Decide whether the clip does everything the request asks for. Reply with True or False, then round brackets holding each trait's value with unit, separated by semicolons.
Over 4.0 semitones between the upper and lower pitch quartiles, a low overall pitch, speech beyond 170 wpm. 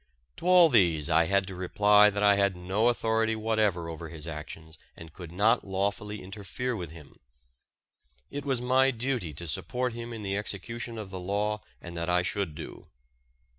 True (4.4 semitones; 100 Hz; 180 wpm)